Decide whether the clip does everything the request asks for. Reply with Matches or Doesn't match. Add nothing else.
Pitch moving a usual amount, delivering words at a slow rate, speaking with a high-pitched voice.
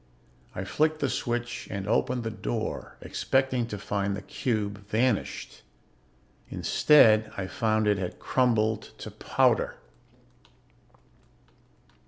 Doesn't match